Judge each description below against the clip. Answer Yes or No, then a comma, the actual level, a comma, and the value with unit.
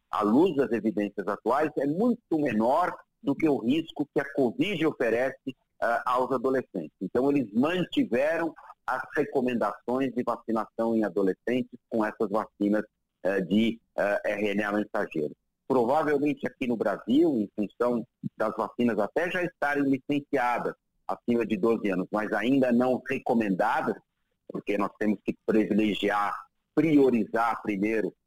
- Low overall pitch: Yes, low, 120 Hz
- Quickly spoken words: No, average, 135 wpm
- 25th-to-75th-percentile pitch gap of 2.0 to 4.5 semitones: No, average, 5.1 semitones